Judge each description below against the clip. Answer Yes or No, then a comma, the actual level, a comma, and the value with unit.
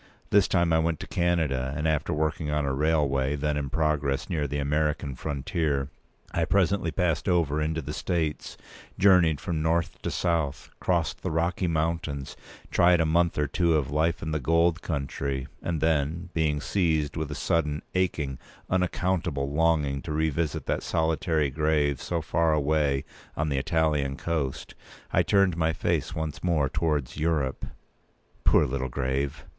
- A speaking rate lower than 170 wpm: Yes, average, 160 wpm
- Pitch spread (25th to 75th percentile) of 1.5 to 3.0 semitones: Yes, narrow, 2.6 semitones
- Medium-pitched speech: No, very low, 80 Hz